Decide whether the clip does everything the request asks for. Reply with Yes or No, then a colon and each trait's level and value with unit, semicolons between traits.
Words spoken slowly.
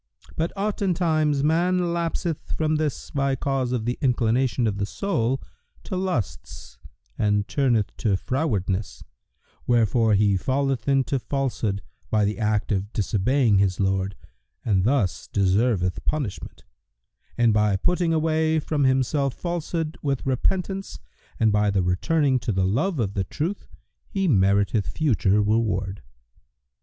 Yes: slow, 130 wpm